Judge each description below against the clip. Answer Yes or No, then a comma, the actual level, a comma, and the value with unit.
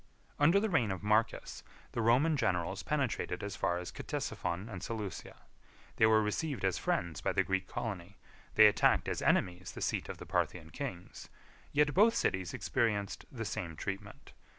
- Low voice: Yes, low, 105 Hz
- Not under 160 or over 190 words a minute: Yes, average, 175 wpm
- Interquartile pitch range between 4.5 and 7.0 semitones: Yes, average, 5.1 semitones